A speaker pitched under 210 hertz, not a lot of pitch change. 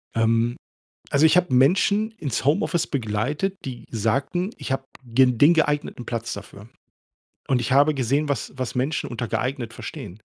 No: low, 135 Hz; average, 4.2 semitones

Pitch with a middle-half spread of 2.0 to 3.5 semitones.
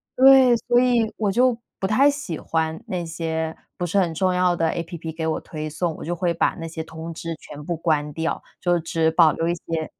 Yes: average, 3.0 semitones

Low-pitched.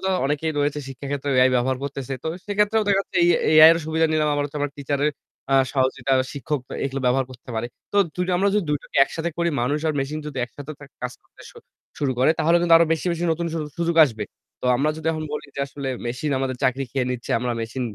No: medium, 145 Hz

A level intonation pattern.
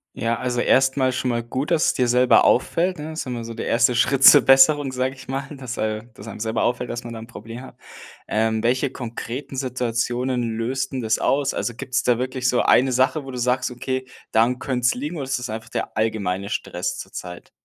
Yes: narrow, 2.3 semitones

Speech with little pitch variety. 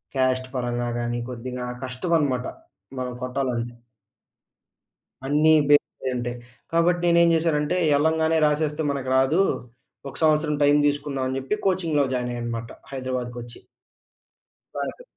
No: average, 3.8 semitones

